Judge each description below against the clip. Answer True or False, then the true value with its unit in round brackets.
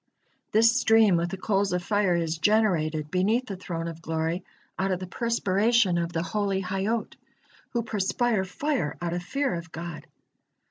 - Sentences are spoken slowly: False (170 wpm)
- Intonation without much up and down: False (4.2 semitones)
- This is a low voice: False (190 Hz)